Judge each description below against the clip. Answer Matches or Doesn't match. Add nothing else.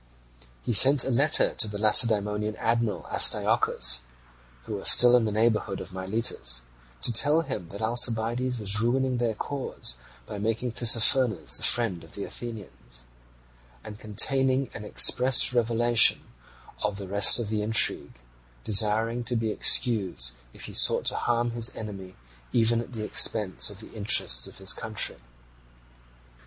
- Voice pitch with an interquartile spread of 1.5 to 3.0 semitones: Matches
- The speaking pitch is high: Doesn't match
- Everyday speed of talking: Matches